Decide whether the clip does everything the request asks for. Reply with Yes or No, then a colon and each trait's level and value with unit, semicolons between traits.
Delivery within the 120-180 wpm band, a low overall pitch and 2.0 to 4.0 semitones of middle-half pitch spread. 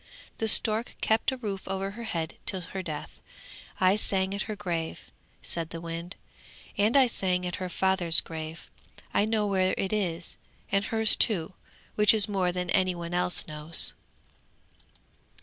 No: average, 165 wpm; high, 190 Hz; average, 3.5 semitones